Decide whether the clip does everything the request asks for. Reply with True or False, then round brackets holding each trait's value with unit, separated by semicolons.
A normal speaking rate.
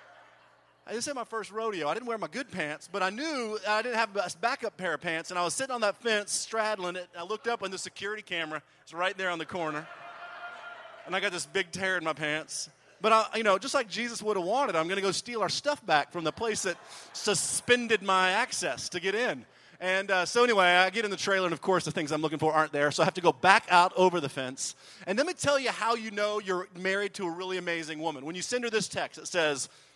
False (270 wpm)